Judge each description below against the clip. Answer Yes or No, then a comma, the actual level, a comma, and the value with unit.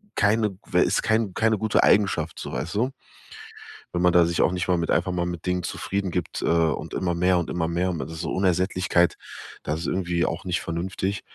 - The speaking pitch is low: Yes, very low, 90 Hz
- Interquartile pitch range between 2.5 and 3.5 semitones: No, narrow, 2.1 semitones